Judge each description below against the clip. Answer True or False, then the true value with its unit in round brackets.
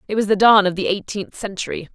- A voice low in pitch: False (200 Hz)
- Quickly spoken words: True (245 wpm)